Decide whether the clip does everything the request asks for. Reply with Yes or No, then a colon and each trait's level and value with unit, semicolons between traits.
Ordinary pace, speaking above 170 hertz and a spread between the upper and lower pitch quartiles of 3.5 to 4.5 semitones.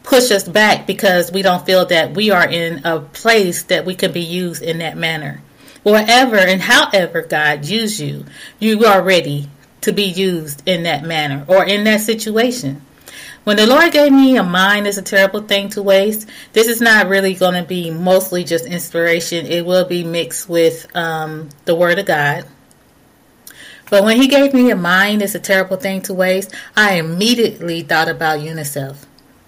Yes: average, 185 wpm; medium, 185 Hz; average, 4.0 semitones